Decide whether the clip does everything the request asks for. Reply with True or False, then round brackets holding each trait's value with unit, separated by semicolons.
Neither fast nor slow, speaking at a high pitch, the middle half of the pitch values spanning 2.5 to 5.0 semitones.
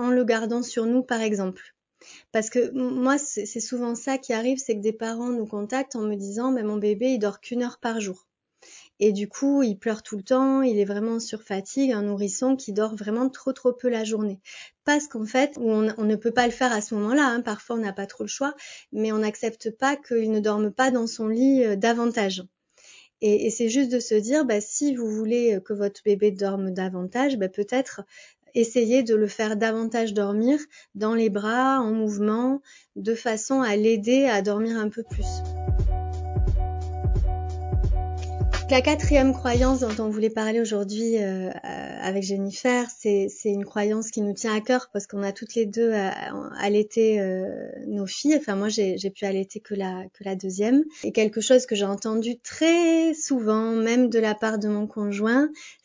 True (200 wpm; 220 Hz; 3.3 semitones)